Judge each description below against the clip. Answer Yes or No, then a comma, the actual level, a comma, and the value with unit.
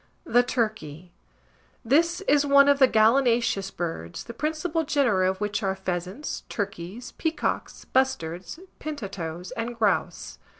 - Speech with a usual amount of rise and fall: No, wide, 6.9 semitones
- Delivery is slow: Yes, slow, 125 wpm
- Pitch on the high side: Yes, high, 225 Hz